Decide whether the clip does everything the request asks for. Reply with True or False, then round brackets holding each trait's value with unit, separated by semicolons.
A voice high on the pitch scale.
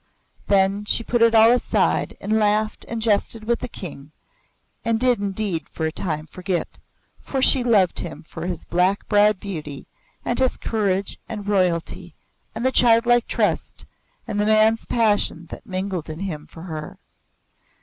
True (205 Hz)